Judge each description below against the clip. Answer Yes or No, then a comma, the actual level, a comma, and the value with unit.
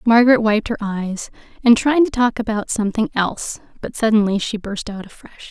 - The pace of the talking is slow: No, average, 185 wpm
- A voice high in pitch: Yes, high, 220 Hz